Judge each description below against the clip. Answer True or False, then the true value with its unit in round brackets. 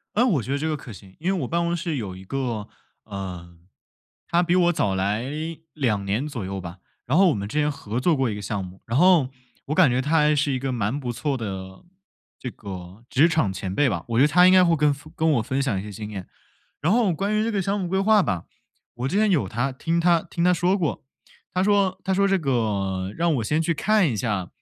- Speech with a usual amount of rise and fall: False (8.8 semitones)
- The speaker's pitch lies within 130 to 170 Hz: True (135 Hz)